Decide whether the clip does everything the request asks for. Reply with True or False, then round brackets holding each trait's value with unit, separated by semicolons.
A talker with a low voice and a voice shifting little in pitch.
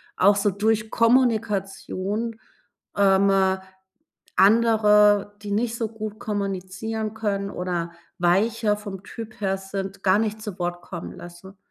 False (205 Hz; 2.3 semitones)